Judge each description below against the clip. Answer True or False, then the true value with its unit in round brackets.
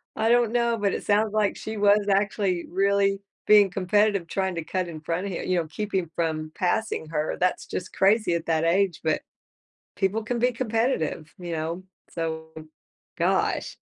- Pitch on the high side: True (195 Hz)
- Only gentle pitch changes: False (4.0 semitones)